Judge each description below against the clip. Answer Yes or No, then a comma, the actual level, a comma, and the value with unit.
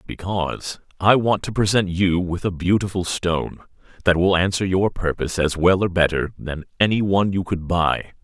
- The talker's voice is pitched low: Yes, very low, 90 Hz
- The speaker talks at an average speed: Yes, average, 180 wpm